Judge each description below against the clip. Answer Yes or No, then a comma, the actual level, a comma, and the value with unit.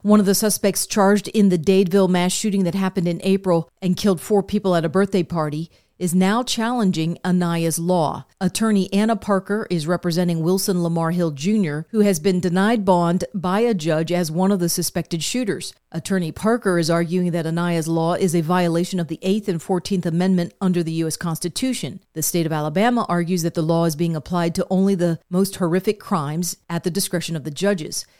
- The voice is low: No, medium, 180 Hz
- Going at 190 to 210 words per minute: Yes, average, 200 wpm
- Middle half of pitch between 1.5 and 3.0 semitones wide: Yes, narrow, 2.5 semitones